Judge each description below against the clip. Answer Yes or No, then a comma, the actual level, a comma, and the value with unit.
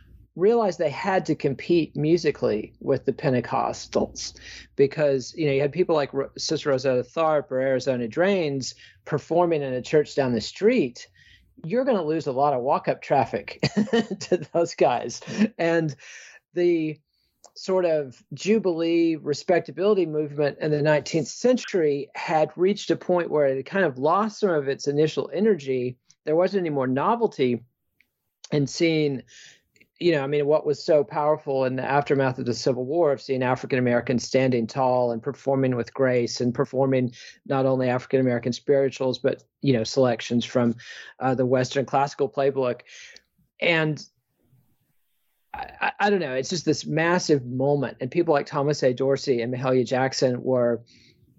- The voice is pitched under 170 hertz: Yes, medium, 140 Hz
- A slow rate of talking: No, average, 160 wpm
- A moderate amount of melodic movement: Yes, average, 4.2 semitones